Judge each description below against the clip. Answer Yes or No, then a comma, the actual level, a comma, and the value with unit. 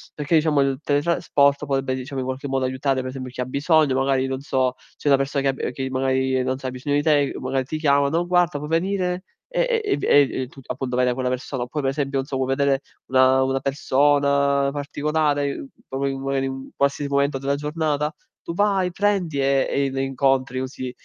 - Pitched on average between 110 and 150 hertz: Yes, medium, 140 Hz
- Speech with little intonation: Yes, narrow, 1.8 semitones